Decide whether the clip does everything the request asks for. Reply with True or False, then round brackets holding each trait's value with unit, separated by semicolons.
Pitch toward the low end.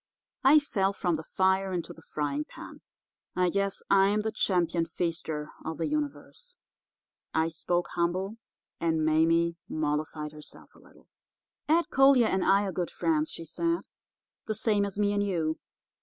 False (185 Hz)